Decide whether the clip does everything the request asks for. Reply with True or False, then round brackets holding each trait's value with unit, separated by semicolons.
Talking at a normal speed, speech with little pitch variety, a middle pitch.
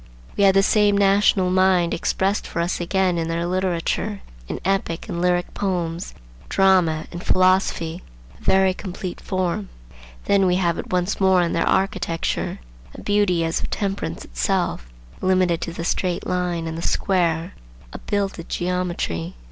True (155 wpm; 2.2 semitones; 180 Hz)